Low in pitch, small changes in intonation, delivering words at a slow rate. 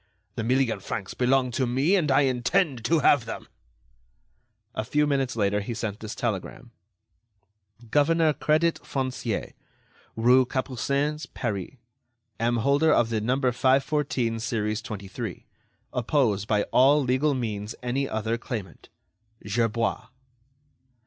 No: low, 125 Hz; average, 3.7 semitones; slow, 120 wpm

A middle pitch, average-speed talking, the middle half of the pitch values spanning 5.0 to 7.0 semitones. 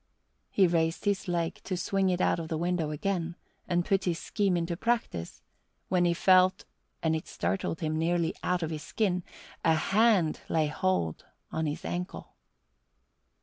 No: medium, 175 Hz; average, 165 wpm; narrow, 2.6 semitones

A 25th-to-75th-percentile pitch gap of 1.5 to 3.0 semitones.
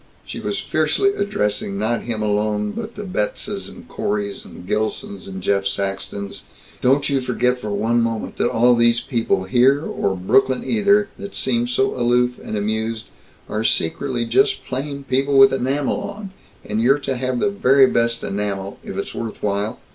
No: average, 4.5 semitones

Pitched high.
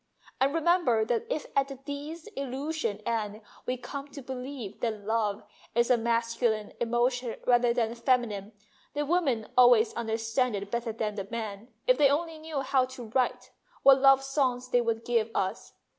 Yes: high, 245 Hz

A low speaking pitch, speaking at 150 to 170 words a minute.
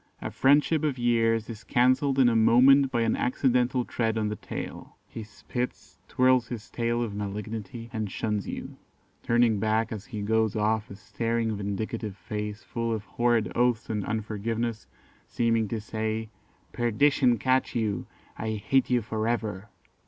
Yes: low, 115 Hz; average, 160 wpm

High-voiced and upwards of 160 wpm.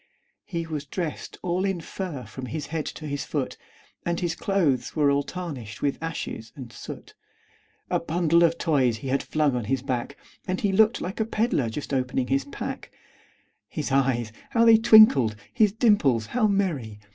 No: medium, 150 Hz; average, 180 wpm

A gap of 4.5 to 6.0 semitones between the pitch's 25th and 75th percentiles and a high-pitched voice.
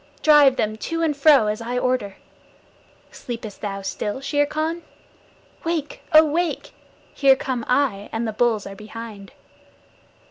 Yes: wide, 5.5 semitones; very high, 250 Hz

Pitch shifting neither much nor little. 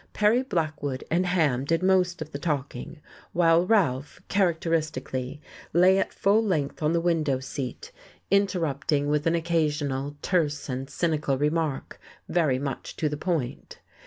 Yes: average, 3.6 semitones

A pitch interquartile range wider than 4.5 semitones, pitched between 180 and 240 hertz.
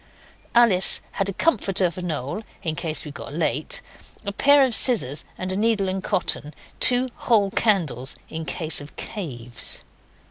Yes: wide, 5.6 semitones; medium, 185 Hz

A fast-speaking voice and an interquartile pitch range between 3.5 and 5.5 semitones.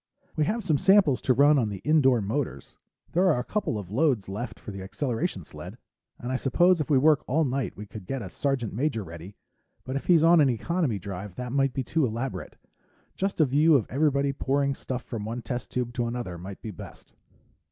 Yes: fast, 215 wpm; average, 5.2 semitones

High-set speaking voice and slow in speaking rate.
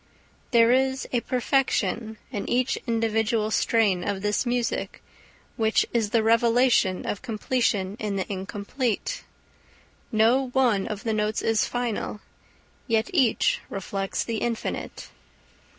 Yes: high, 225 Hz; slow, 120 wpm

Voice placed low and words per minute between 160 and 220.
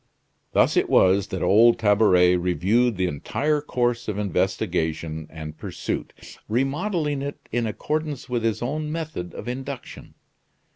No: low, 115 Hz; slow, 135 wpm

